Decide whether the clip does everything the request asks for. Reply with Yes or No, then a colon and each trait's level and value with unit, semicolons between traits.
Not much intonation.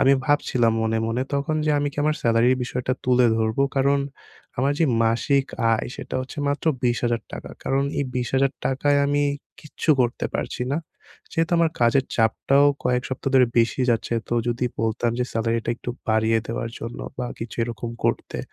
No: average, 3.1 semitones